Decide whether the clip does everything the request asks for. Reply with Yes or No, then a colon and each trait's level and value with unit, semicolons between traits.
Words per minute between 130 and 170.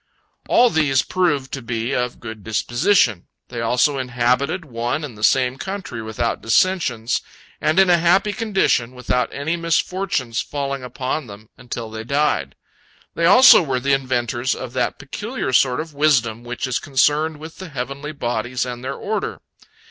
Yes: average, 160 wpm